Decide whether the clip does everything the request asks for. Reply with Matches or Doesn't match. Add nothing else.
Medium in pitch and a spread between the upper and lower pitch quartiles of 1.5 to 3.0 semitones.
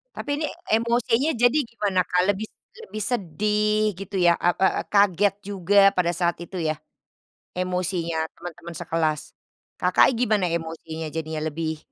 Doesn't match